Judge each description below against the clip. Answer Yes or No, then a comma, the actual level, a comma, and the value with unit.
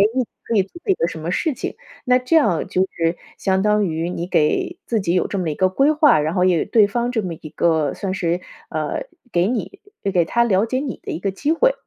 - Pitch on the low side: No, high, 195 Hz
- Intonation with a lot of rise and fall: Yes, wide, 6.6 semitones